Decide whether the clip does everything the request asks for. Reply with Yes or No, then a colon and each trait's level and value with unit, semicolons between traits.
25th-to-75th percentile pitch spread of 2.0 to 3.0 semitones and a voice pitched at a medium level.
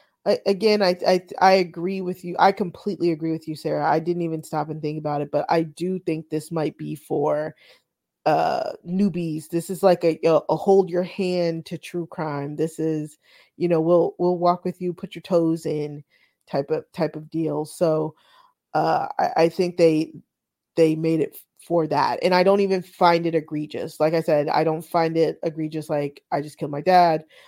Yes: narrow, 2.4 semitones; medium, 165 Hz